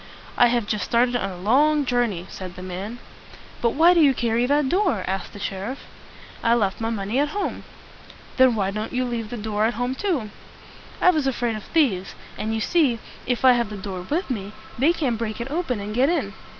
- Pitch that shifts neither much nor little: Yes, average, 4.4 semitones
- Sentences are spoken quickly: Yes, fast, 220 wpm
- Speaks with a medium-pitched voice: No, high, 235 Hz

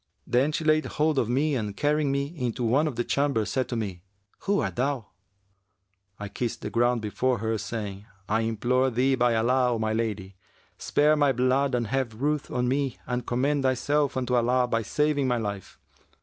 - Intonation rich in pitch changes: No, average, 3.5 semitones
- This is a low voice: Yes, low, 125 Hz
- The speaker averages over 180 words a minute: Yes, average, 190 wpm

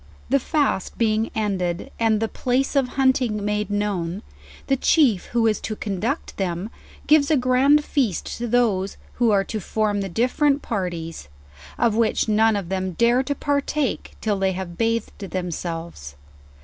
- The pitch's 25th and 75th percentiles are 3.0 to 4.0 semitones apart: No, average, 4.8 semitones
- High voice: Yes, high, 220 Hz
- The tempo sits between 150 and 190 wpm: Yes, average, 160 wpm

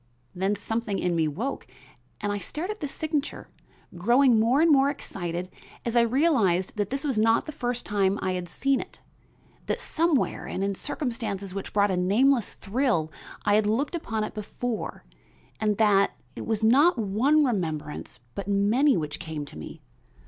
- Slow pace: No, average, 175 wpm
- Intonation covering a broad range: Yes, wide, 5.7 semitones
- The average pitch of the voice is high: Yes, high, 215 Hz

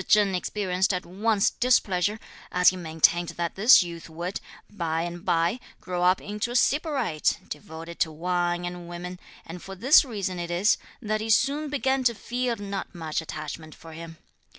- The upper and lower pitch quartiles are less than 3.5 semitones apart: No, average, 3.8 semitones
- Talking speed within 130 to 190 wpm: Yes, average, 175 wpm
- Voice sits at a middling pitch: Yes, medium, 180 Hz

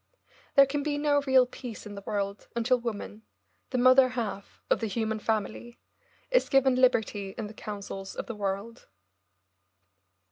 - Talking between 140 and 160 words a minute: Yes, average, 155 wpm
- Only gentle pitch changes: No, average, 3.7 semitones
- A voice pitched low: No, high, 230 Hz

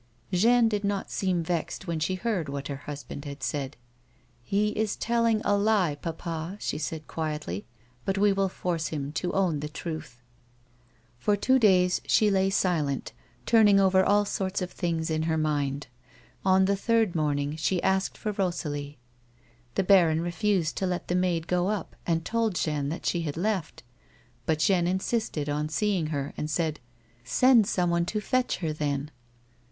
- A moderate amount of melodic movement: Yes, average, 4.5 semitones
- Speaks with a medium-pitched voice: Yes, medium, 175 Hz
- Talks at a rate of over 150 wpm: Yes, average, 175 wpm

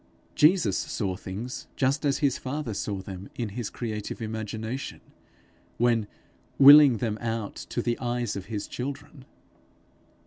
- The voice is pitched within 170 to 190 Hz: No, low, 115 Hz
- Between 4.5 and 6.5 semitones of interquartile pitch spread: No, average, 4.1 semitones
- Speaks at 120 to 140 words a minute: Yes, slow, 135 wpm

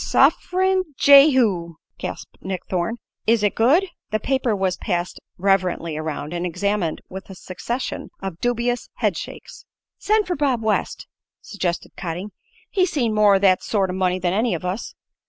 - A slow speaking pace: No, average, 160 wpm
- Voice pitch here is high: Yes, high, 200 Hz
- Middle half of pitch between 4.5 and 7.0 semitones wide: Yes, average, 5.2 semitones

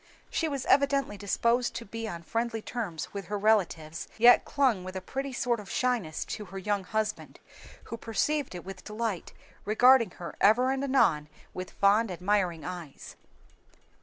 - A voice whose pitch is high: Yes, high, 215 Hz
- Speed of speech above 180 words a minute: No, average, 165 wpm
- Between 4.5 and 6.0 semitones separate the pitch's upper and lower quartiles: Yes, average, 4.8 semitones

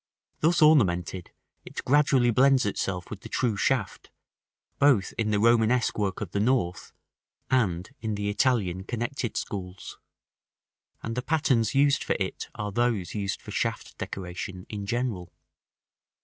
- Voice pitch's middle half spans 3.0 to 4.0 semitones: No, average, 4.8 semitones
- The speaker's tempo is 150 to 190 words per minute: No, average, 140 wpm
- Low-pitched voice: Yes, low, 110 Hz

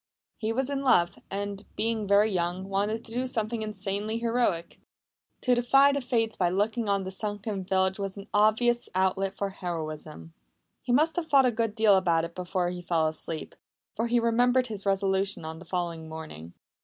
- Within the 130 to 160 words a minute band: No, average, 185 wpm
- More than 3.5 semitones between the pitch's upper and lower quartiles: Yes, average, 4.2 semitones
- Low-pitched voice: No, high, 200 Hz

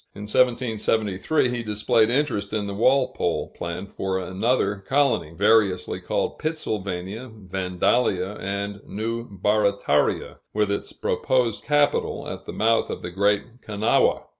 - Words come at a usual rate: No, slow, 125 wpm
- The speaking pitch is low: Yes, low, 105 Hz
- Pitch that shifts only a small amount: No, average, 3.3 semitones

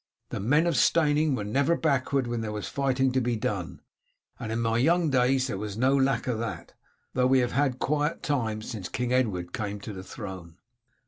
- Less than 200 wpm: No, fast, 205 wpm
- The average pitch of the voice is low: Yes, low, 125 Hz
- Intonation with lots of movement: No, average, 4.1 semitones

